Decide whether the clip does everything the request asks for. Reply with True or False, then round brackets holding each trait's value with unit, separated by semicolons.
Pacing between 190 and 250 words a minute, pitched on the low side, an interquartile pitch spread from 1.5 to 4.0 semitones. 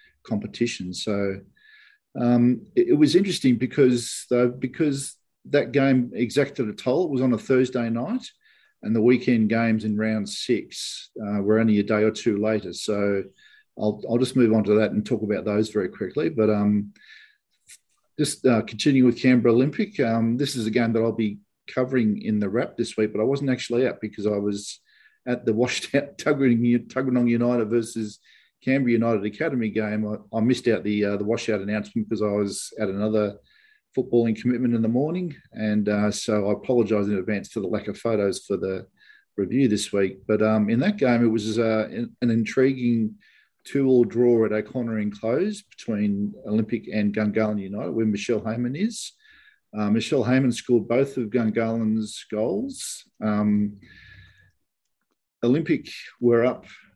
False (175 wpm; 115 Hz; 3.2 semitones)